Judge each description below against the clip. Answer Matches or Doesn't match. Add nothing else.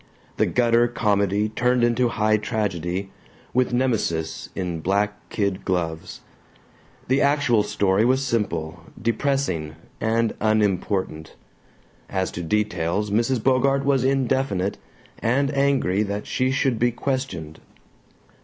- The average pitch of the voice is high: Doesn't match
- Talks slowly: Matches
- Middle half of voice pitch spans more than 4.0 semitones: Matches